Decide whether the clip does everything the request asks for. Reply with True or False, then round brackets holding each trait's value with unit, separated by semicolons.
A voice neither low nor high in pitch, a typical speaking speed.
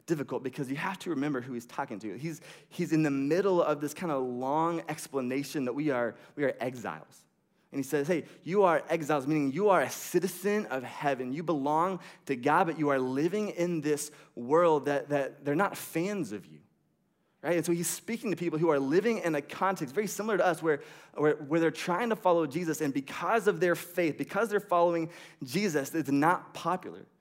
False (165 Hz; 210 wpm)